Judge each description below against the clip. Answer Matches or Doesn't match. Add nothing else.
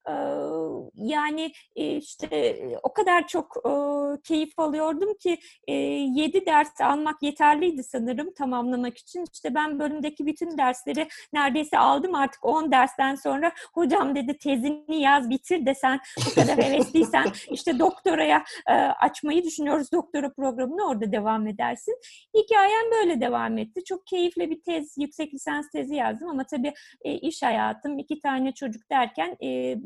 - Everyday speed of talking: Matches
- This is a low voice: Doesn't match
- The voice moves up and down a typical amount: Matches